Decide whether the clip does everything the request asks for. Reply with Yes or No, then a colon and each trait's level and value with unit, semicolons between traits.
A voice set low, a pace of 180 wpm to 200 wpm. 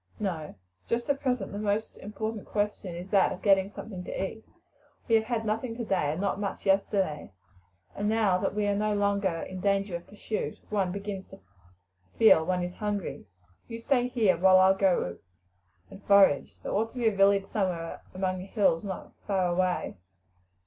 No: high, 200 Hz; average, 185 wpm